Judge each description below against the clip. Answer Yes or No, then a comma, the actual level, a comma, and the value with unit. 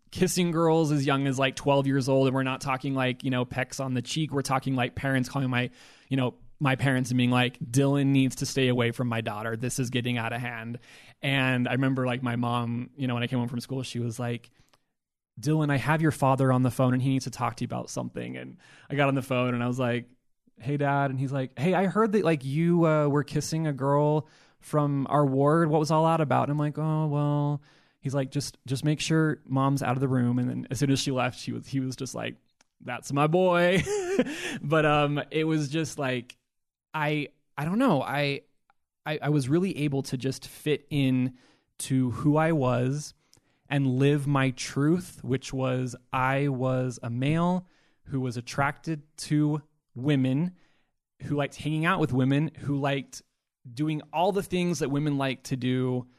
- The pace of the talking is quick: Yes, fast, 215 wpm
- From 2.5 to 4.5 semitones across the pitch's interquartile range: Yes, average, 2.9 semitones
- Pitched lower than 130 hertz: No, low, 135 Hz